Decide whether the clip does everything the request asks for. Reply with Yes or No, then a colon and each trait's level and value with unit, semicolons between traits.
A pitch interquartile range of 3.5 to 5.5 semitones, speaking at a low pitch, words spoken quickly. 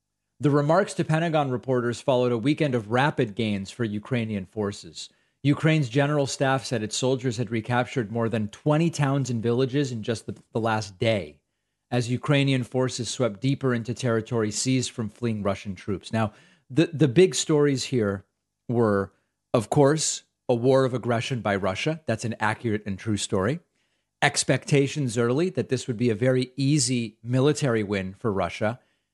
No: average, 4.1 semitones; low, 125 Hz; average, 165 wpm